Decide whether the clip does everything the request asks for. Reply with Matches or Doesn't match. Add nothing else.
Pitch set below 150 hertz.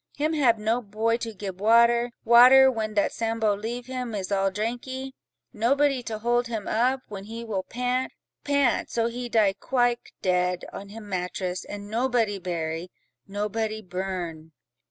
Doesn't match